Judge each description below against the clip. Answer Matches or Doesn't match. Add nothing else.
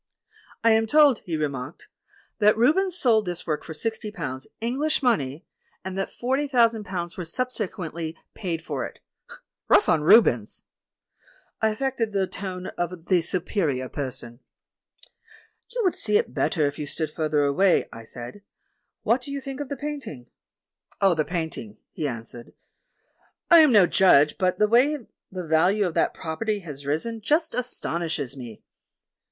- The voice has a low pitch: Doesn't match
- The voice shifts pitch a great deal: Matches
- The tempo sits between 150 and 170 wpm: Matches